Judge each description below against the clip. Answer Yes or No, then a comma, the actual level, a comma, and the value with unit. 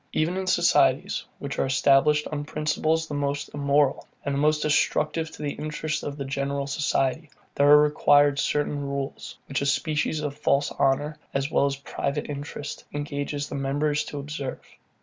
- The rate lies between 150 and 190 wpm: Yes, average, 170 wpm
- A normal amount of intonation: No, narrow, 1.3 semitones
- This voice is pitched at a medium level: Yes, medium, 145 Hz